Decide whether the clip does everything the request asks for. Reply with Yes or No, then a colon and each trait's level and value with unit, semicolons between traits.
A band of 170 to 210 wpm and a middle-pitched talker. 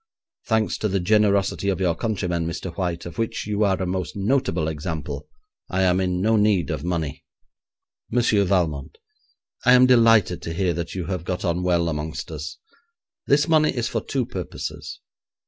No: average, 175 wpm; very low, 95 Hz